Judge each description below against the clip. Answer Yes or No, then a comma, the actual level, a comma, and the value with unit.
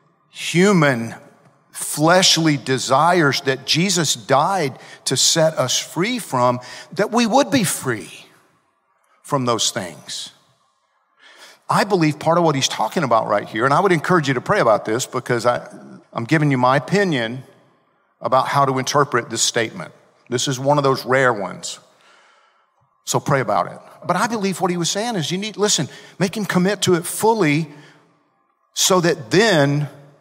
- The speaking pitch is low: No, medium, 155 Hz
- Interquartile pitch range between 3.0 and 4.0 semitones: No, average, 5.3 semitones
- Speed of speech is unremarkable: Yes, average, 165 wpm